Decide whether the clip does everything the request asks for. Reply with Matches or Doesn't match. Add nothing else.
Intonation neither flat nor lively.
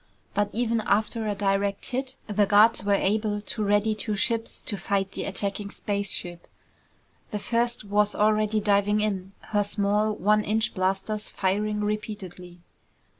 Doesn't match